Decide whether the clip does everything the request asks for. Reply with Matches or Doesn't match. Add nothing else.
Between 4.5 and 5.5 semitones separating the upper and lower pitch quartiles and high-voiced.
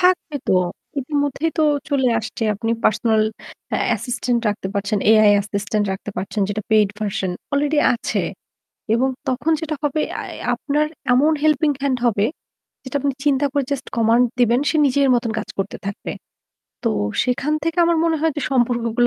Matches